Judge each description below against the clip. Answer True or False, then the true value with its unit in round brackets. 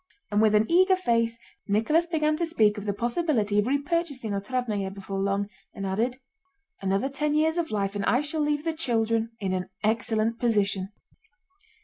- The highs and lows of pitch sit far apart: True (6.5 semitones)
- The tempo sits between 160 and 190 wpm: True (170 wpm)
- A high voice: True (230 Hz)